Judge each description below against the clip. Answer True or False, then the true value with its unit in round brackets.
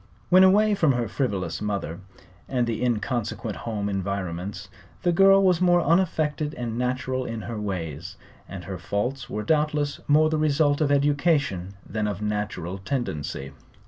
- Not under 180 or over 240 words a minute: False (150 wpm)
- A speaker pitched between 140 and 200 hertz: False (120 Hz)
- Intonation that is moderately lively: False (7.1 semitones)